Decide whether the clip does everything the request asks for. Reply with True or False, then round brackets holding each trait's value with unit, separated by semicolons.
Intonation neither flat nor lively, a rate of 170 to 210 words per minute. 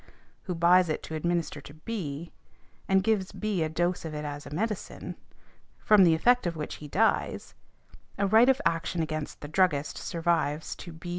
True (3.7 semitones; 180 wpm)